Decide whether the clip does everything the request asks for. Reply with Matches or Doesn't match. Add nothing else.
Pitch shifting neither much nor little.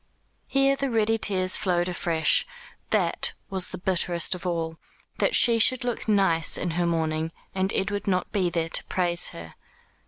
Matches